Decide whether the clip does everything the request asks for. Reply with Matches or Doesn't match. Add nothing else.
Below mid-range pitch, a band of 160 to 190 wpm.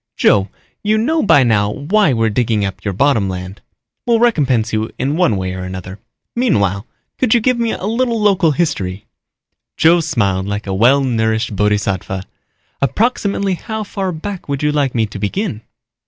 Matches